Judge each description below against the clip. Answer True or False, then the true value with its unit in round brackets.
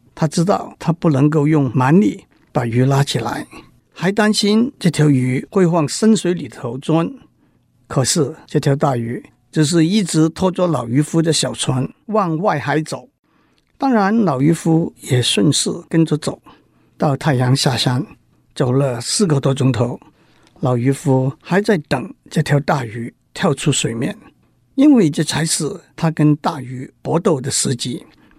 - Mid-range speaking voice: True (150 Hz)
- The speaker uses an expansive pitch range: False (4.1 semitones)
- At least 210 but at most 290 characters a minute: True (215 characters per minute)